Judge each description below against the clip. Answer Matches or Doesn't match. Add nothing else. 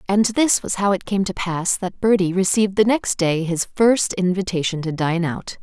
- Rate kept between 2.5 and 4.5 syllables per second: Doesn't match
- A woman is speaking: Matches